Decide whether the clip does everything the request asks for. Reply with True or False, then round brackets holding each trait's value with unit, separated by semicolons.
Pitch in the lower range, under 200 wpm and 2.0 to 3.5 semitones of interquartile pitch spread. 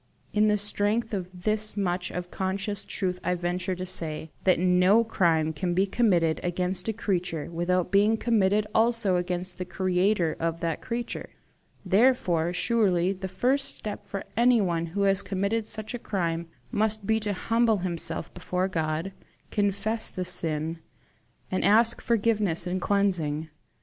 False (190 Hz; 150 wpm; 3.2 semitones)